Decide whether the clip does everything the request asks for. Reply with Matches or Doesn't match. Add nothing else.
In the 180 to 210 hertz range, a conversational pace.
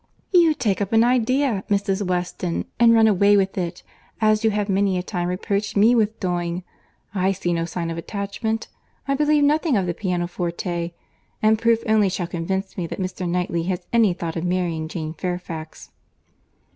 Matches